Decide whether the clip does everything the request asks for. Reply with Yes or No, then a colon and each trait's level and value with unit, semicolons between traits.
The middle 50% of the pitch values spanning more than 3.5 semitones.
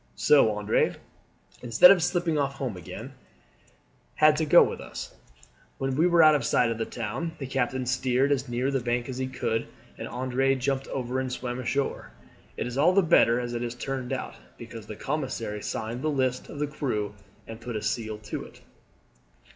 No: average, 3.0 semitones